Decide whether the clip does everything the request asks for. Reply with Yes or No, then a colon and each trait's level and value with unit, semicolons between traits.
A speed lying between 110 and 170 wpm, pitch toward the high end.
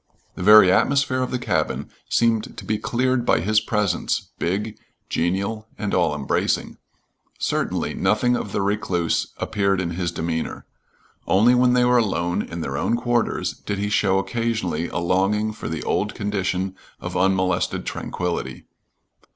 No: average, 150 wpm; low, 100 Hz